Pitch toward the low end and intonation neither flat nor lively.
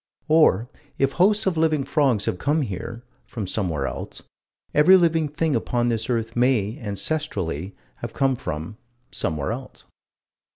No: low, 125 Hz; wide, 7.2 semitones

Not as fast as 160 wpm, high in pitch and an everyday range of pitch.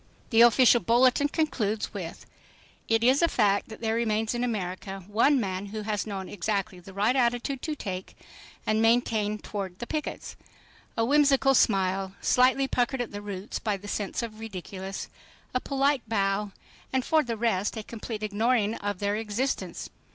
No: average, 165 wpm; high, 220 Hz; average, 3.4 semitones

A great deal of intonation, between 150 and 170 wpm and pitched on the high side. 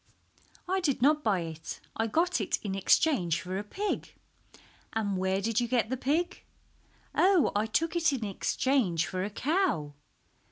Yes: wide, 8.4 semitones; average, 165 wpm; high, 225 Hz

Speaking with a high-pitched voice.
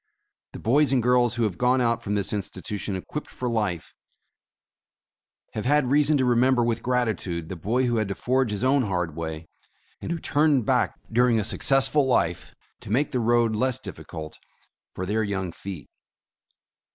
No: low, 115 Hz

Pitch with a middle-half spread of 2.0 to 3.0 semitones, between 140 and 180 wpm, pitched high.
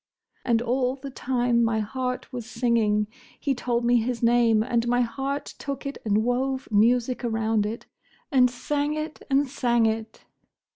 Yes: narrow, 2.4 semitones; average, 155 wpm; high, 245 Hz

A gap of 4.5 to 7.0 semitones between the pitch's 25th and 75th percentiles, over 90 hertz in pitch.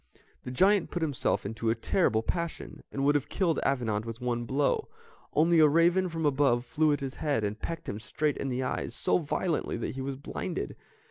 Yes: average, 5.1 semitones; medium, 140 Hz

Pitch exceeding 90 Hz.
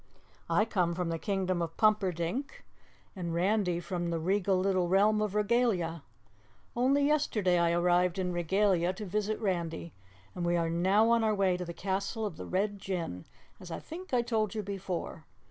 Yes: high, 190 Hz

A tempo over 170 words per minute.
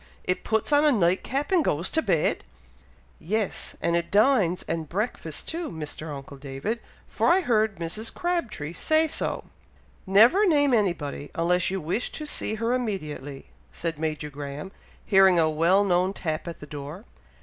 No: average, 165 wpm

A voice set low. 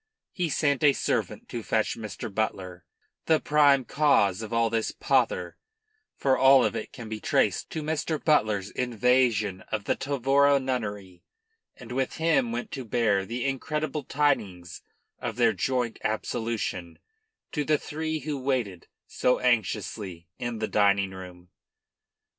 Yes: low, 120 Hz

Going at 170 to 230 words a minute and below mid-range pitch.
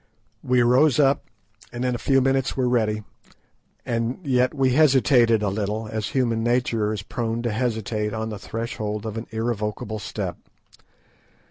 No: average, 155 wpm; low, 115 Hz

